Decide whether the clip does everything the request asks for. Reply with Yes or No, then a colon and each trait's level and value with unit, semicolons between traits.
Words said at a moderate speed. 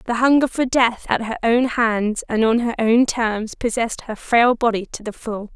No: fast, 215 wpm